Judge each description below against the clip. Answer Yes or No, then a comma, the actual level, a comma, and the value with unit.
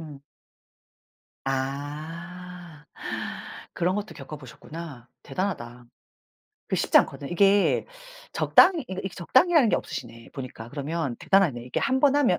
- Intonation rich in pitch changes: Yes, wide, 6.0 semitones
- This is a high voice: No, medium, 165 Hz